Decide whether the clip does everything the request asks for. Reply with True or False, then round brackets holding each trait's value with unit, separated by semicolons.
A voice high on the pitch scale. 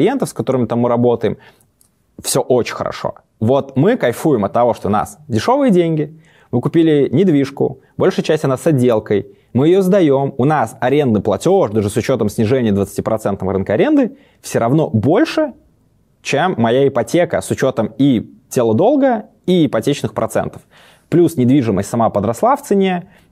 False (140 Hz)